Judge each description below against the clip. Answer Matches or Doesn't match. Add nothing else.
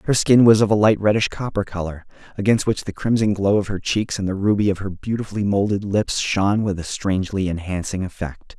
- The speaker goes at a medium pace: Doesn't match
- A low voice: Matches